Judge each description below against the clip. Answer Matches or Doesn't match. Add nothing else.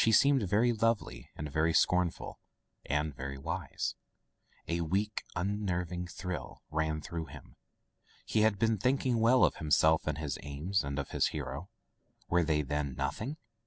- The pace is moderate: Matches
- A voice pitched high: Doesn't match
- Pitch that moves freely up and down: Matches